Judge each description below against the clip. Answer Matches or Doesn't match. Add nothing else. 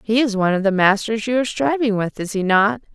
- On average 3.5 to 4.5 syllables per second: Doesn't match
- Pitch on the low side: Doesn't match